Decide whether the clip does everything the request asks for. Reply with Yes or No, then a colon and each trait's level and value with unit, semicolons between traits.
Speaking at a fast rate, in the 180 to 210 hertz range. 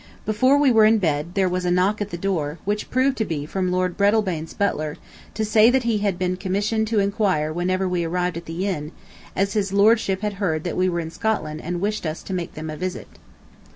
Yes: fast, 230 wpm; medium, 185 Hz